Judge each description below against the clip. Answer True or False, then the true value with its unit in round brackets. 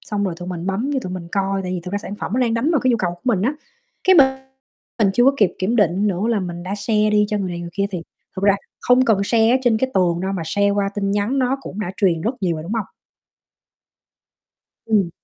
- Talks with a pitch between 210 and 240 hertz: False (200 Hz)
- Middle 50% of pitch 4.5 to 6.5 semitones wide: False (3.8 semitones)